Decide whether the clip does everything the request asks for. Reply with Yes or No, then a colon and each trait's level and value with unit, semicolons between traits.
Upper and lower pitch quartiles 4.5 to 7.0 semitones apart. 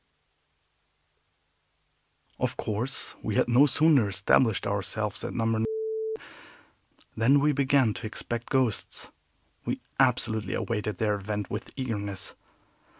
No: average, 4.0 semitones